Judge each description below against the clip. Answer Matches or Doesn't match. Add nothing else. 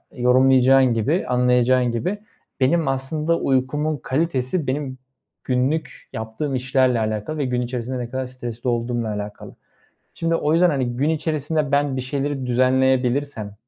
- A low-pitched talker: Matches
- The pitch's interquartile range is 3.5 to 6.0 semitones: Doesn't match